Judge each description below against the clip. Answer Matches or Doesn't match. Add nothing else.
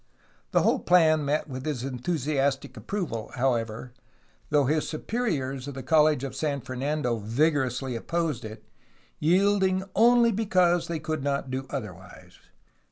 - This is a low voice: Doesn't match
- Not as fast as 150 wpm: Matches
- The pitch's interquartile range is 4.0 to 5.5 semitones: Matches